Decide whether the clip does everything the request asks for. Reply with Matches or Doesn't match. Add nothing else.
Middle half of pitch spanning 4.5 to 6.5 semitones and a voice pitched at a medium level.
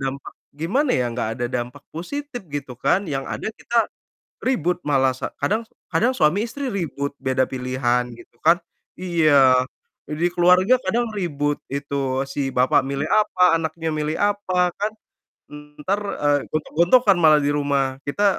Matches